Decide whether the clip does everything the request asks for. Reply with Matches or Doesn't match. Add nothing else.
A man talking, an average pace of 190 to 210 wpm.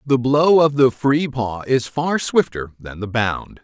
Matches